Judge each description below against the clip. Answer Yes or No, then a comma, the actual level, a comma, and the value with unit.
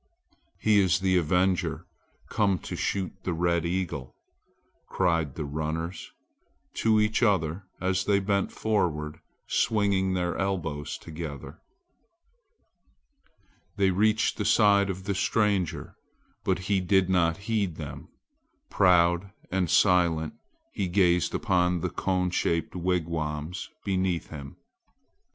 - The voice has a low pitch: Yes, very low, 90 Hz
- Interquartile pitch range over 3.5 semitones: No, average, 2.8 semitones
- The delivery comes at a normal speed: No, slow, 115 wpm